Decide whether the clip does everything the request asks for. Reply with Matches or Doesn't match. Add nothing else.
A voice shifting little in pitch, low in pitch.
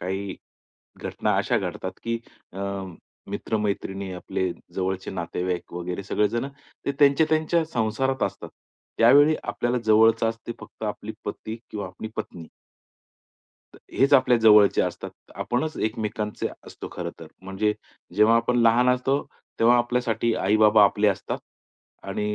Doesn't match